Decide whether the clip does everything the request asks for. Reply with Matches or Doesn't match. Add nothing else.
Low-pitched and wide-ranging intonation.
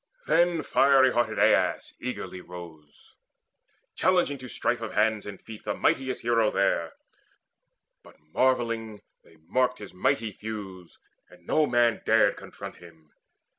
Matches